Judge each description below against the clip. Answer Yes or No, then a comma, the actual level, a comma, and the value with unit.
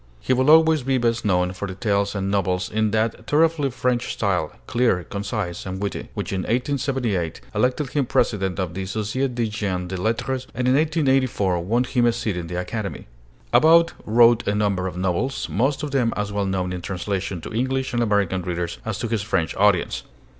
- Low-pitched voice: Yes, low, 105 Hz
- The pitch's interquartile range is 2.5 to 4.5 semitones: No, average, 5.2 semitones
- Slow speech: No, average, 195 wpm